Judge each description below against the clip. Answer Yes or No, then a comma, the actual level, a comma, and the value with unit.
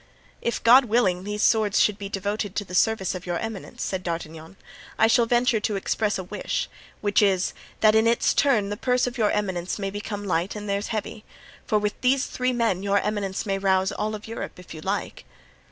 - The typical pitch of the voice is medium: No, high, 205 Hz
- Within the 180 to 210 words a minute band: Yes, average, 200 wpm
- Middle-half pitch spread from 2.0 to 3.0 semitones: Yes, narrow, 2.6 semitones